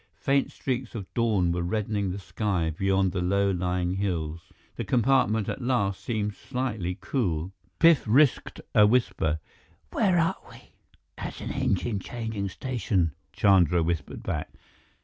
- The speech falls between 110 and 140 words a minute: Yes, slow, 135 wpm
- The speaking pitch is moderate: No, low, 100 Hz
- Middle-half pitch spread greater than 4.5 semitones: Yes, average, 5.0 semitones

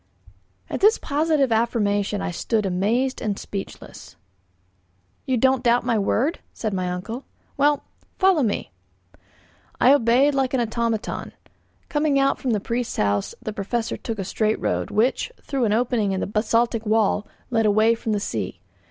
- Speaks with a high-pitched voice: Yes, high, 230 Hz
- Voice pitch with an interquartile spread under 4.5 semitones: Yes, average, 3.9 semitones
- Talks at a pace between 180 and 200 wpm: No, average, 160 wpm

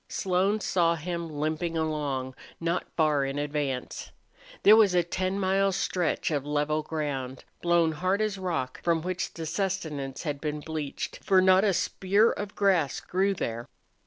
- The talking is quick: No, average, 160 wpm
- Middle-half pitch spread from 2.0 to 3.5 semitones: No, average, 4.1 semitones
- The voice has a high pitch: No, medium, 165 Hz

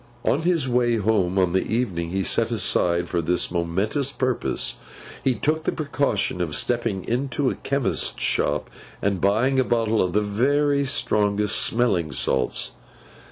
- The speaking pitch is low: Yes, low, 110 Hz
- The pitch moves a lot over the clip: Yes, wide, 6.2 semitones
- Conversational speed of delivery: Yes, average, 155 wpm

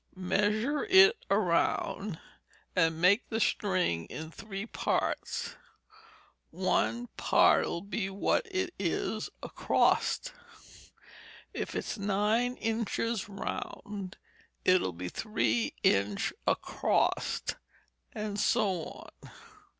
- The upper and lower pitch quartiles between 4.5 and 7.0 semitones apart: No, average, 3.8 semitones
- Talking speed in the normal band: No, slow, 95 wpm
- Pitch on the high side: Yes, high, 200 Hz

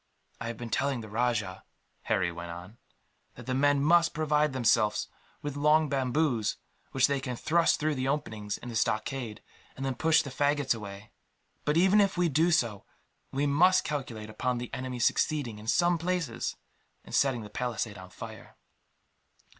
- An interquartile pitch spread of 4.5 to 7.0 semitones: Yes, average, 5.1 semitones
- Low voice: Yes, low, 130 Hz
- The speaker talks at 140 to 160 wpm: No, average, 170 wpm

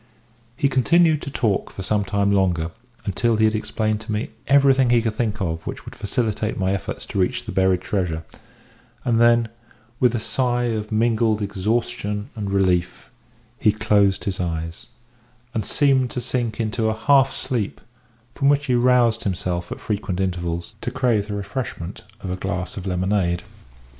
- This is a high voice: No, low, 105 Hz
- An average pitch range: Yes, average, 3.9 semitones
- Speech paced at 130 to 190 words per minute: Yes, average, 170 wpm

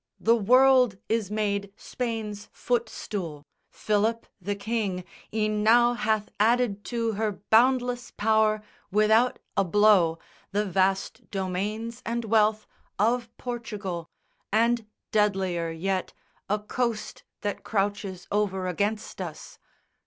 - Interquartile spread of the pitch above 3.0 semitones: No, narrow, 2.6 semitones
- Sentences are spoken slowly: Yes, slow, 110 wpm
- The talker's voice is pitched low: No, high, 215 Hz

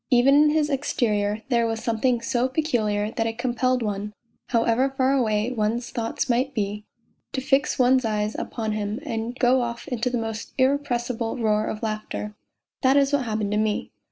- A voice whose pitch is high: Yes, high, 235 Hz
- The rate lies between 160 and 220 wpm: Yes, average, 180 wpm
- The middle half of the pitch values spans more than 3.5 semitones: No, average, 3.2 semitones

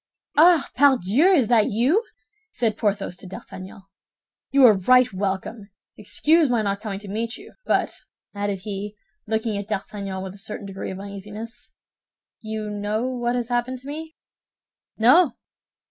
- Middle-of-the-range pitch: No, high, 220 Hz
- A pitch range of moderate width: Yes, average, 4.0 semitones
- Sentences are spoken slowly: No, average, 150 wpm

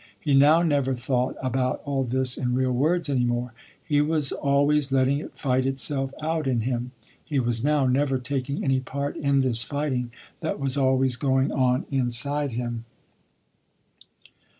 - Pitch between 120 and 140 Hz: Yes, low, 135 Hz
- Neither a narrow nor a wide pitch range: No, narrow, 2.1 semitones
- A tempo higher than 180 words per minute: No, average, 160 wpm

